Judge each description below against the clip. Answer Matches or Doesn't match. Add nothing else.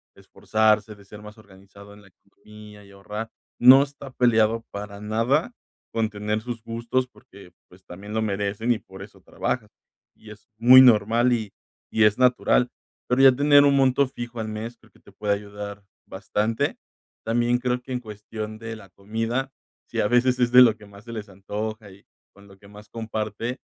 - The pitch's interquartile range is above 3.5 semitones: Doesn't match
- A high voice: Doesn't match